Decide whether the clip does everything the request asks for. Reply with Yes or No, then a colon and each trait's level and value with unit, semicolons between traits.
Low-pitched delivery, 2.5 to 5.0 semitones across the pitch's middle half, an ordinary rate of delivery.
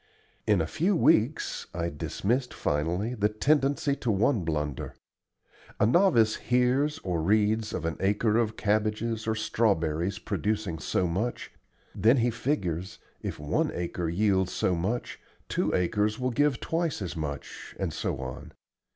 No: low, 105 Hz; wide, 5.6 semitones; average, 145 wpm